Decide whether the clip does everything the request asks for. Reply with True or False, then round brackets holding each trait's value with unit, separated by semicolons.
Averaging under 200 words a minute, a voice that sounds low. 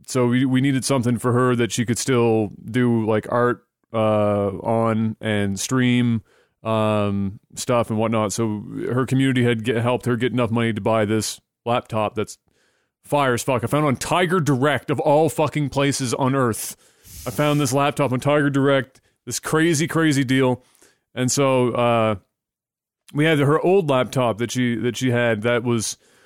True (180 wpm; 125 Hz)